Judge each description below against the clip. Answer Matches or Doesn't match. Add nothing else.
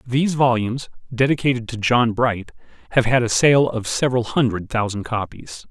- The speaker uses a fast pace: Doesn't match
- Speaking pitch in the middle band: Doesn't match